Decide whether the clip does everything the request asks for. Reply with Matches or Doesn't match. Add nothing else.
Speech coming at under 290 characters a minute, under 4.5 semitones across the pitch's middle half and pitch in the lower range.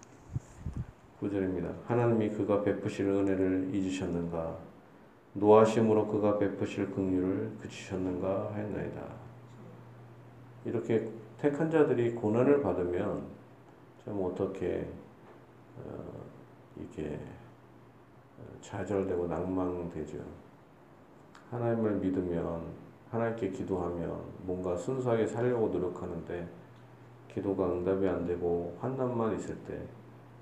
Matches